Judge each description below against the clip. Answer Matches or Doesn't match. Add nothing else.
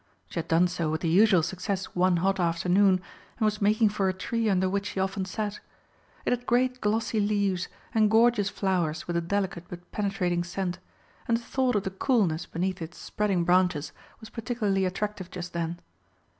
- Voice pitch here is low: Doesn't match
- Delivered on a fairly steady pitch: Doesn't match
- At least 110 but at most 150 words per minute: Doesn't match